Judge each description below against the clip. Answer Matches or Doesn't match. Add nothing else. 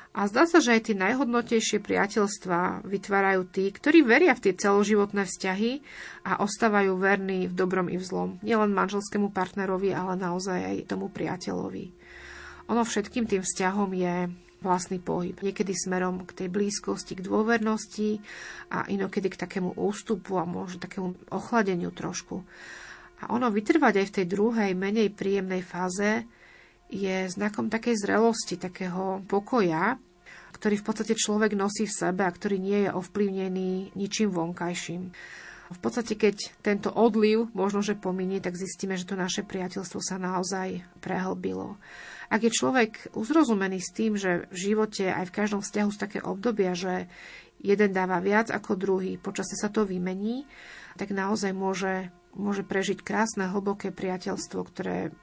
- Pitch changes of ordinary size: Doesn't match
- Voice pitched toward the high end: Matches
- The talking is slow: Doesn't match